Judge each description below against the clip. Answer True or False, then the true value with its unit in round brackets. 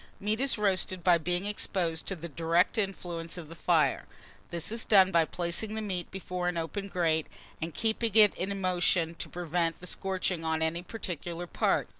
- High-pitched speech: False (180 Hz)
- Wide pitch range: False (2.8 semitones)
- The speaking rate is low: False (185 wpm)